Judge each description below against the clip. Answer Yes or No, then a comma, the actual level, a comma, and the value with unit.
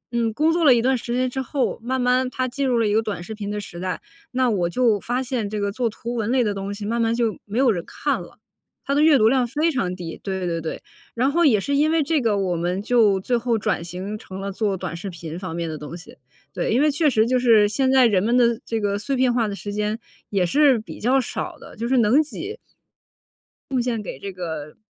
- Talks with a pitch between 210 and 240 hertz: Yes, high, 230 Hz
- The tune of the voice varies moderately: Yes, average, 4.3 semitones